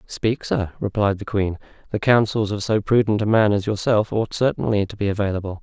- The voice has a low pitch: Yes, low, 105 Hz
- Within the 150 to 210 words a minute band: Yes, fast, 205 wpm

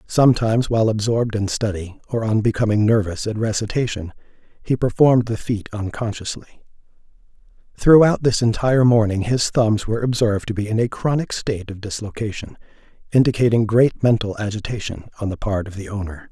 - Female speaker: No, male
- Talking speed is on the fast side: No, average, 155 wpm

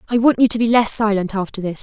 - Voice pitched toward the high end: Yes, high, 215 Hz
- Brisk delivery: Yes, fast, 295 wpm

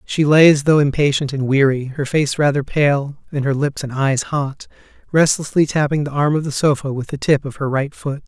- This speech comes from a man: Yes, male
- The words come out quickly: Yes, fast, 225 wpm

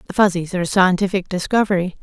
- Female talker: Yes, female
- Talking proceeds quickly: No, average, 180 wpm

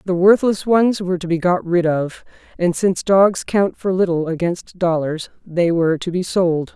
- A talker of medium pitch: Yes, medium, 180 Hz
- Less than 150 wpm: No, average, 195 wpm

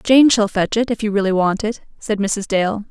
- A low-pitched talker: No, high, 210 Hz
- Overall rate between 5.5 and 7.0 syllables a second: No, 4.9 syllables/s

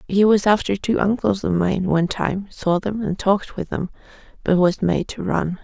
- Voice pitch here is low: No, high, 195 Hz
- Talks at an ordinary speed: No, fast, 215 wpm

